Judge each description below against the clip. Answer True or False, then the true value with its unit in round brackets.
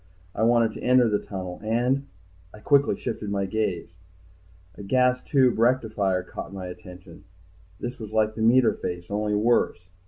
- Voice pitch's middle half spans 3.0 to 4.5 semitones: True (3.8 semitones)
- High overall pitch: False (110 Hz)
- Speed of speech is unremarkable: True (160 wpm)